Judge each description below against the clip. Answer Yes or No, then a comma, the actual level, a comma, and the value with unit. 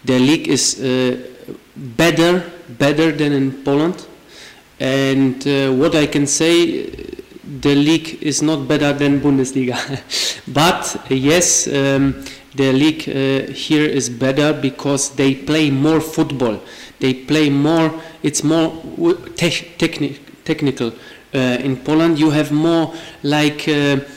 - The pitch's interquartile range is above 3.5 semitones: No, average, 2.9 semitones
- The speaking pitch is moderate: Yes, medium, 145 Hz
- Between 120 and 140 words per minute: Yes, average, 130 wpm